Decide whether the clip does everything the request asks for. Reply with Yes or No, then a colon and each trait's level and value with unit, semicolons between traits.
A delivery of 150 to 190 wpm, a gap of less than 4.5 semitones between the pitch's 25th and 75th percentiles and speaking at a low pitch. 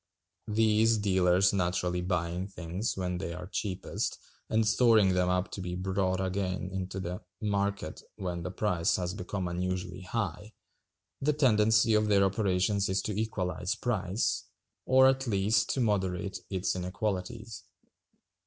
No: average, 140 wpm; average, 2.7 semitones; very low, 95 Hz